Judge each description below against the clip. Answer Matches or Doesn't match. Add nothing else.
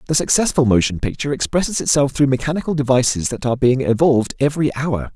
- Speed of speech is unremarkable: Matches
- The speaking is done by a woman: Doesn't match